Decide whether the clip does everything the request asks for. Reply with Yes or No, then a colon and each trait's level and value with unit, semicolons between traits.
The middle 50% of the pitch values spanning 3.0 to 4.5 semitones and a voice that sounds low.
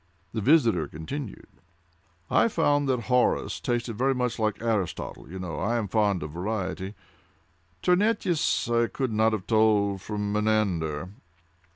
Yes: average, 4.2 semitones; low, 110 Hz